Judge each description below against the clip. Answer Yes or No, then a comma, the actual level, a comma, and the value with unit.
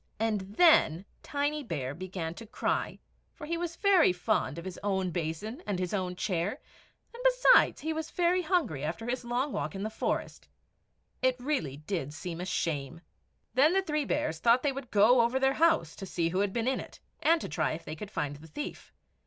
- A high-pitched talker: Yes, high, 215 Hz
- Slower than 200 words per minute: No, fast, 205 wpm